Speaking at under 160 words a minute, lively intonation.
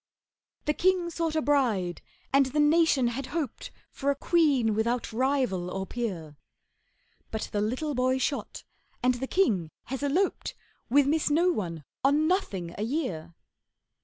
Yes: average, 150 wpm; wide, 5.8 semitones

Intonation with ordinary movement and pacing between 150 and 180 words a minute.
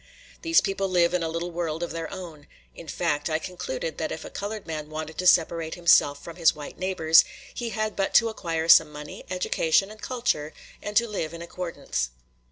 No: average, 3.5 semitones; average, 200 wpm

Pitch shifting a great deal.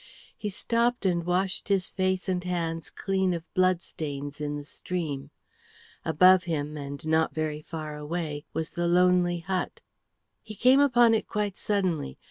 No: average, 3.4 semitones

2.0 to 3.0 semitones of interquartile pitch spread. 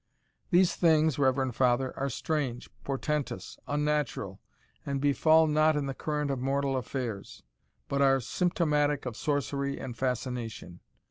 Yes: narrow, 2.5 semitones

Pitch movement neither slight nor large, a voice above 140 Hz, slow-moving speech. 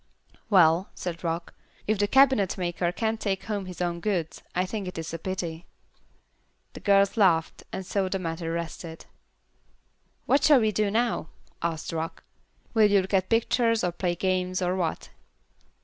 No: average, 3.3 semitones; medium, 185 Hz; average, 165 wpm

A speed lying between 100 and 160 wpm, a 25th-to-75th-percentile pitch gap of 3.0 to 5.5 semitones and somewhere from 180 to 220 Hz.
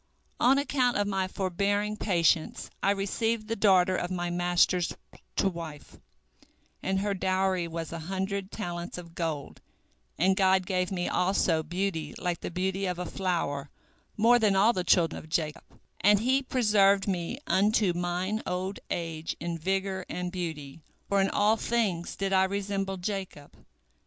No: average, 155 wpm; narrow, 2.4 semitones; high, 190 Hz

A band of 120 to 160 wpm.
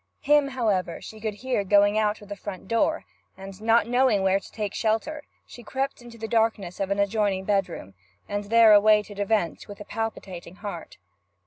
No: average, 185 wpm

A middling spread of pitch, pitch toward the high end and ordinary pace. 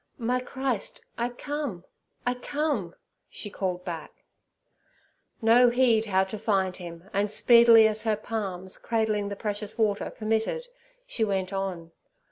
No: average, 3.7 semitones; high, 215 Hz; slow, 130 wpm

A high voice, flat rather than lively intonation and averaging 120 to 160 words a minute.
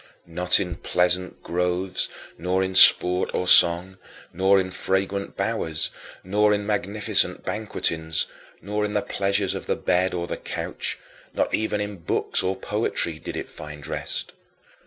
No: very low, 95 Hz; narrow, 2.2 semitones; average, 150 wpm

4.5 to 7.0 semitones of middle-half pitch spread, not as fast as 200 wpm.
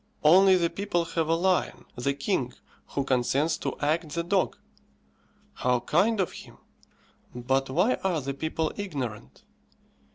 Yes: average, 5.3 semitones; average, 140 wpm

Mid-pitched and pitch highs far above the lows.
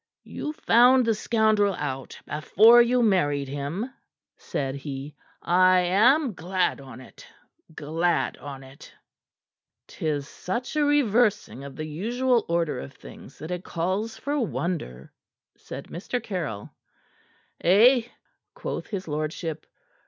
Yes: medium, 180 Hz; wide, 7.8 semitones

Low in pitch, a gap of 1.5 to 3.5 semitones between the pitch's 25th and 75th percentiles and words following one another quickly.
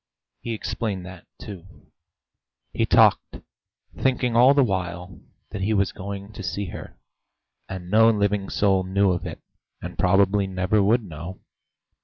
No: low, 100 Hz; narrow, 2.5 semitones; average, 145 wpm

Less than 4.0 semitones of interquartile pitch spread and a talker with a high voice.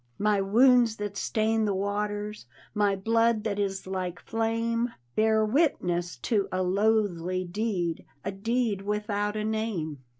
Yes: narrow, 2.5 semitones; high, 210 Hz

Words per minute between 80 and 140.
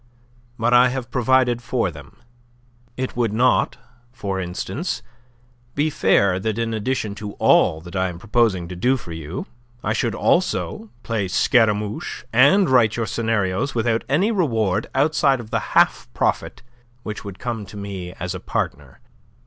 No: average, 155 wpm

